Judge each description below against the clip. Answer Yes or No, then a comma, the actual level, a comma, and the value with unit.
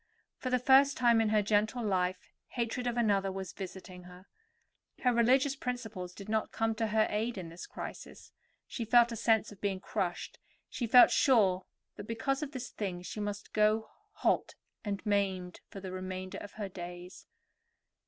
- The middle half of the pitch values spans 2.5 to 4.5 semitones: Yes, average, 3.9 semitones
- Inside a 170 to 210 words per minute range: Yes, average, 175 wpm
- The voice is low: No, high, 210 Hz